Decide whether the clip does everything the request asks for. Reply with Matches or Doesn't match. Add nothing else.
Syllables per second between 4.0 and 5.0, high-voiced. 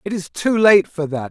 Doesn't match